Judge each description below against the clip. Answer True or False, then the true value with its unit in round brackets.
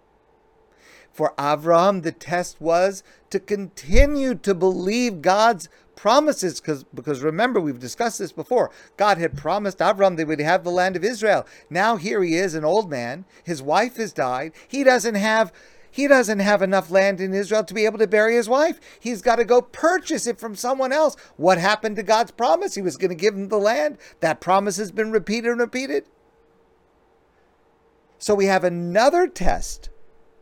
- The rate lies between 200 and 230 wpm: False (180 wpm)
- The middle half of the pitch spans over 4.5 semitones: True (5.2 semitones)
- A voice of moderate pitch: False (215 Hz)